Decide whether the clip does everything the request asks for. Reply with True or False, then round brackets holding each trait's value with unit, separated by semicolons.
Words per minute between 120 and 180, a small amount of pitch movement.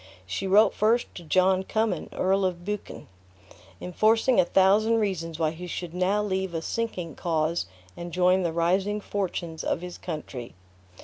False (160 wpm; 3.1 semitones)